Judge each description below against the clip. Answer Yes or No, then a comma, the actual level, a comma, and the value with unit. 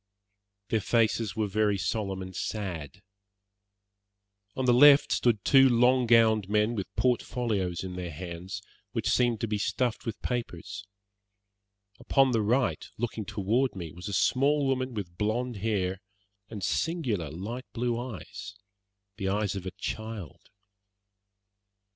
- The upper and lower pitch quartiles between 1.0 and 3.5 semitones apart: No, average, 4.2 semitones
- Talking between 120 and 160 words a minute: Yes, average, 140 wpm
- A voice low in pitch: Yes, low, 110 Hz